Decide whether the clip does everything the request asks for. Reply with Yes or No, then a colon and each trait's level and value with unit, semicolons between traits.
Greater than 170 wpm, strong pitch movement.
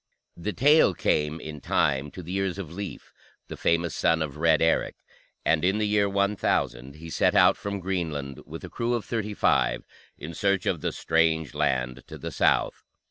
No: average, 190 wpm; average, 4.7 semitones